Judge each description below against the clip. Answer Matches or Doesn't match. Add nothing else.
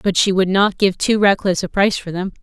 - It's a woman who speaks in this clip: Matches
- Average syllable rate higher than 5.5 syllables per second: Matches